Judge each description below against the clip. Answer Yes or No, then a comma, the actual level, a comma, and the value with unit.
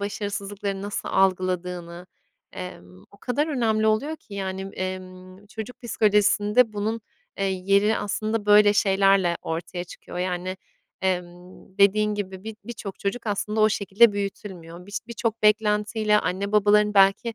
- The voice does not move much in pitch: Yes, narrow, 2.3 semitones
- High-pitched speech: Yes, high, 200 Hz